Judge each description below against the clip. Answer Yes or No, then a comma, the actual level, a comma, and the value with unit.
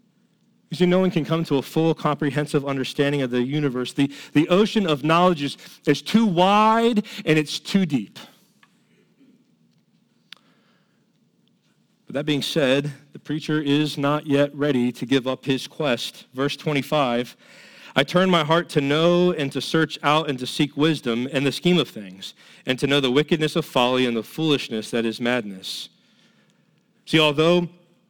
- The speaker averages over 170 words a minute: No, average, 165 wpm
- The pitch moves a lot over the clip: No, average, 3.5 semitones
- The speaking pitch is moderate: Yes, medium, 150 Hz